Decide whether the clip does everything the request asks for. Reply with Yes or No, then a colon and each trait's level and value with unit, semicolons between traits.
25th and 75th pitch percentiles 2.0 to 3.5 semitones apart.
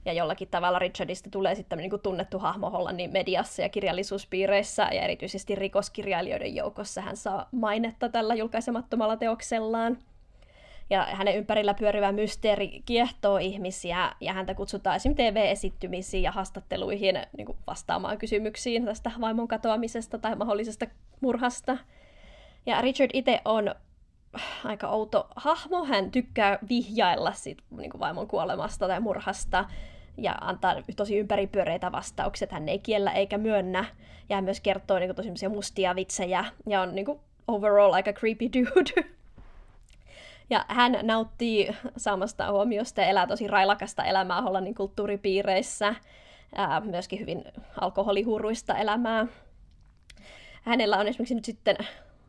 Yes: average, 2.8 semitones